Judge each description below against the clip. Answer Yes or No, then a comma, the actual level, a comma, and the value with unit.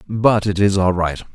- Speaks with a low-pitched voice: Yes, low, 100 Hz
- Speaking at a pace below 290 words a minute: Yes, fast, 225 wpm